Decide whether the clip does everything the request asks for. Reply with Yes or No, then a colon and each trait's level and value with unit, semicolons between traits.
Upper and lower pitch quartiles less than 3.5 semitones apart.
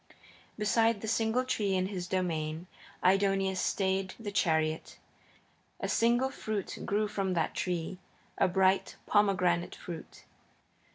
Yes: average, 2.8 semitones